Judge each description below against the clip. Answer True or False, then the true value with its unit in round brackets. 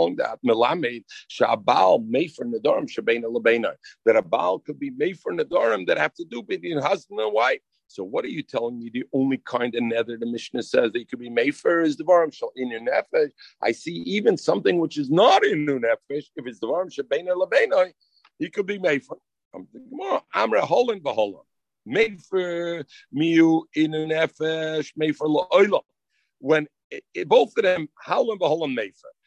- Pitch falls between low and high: True (160 Hz)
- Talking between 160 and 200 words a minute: True (185 wpm)